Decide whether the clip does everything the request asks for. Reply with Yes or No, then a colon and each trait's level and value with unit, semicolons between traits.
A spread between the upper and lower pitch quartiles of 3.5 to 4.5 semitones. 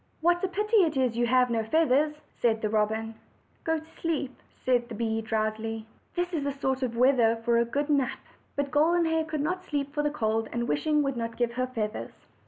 No: average, 5.0 semitones